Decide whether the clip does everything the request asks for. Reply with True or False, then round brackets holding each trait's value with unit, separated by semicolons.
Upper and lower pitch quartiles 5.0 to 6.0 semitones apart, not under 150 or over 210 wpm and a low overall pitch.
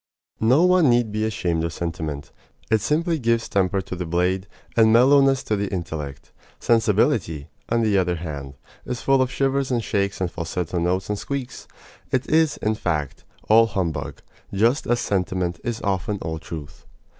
True (5.6 semitones; 170 wpm; 105 Hz)